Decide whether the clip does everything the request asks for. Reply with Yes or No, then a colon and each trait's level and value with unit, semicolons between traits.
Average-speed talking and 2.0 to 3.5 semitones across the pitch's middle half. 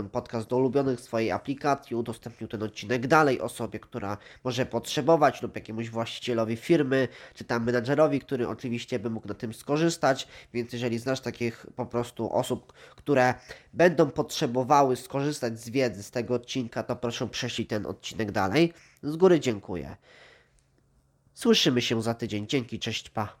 Yes: average, 150 wpm; average, 2.8 semitones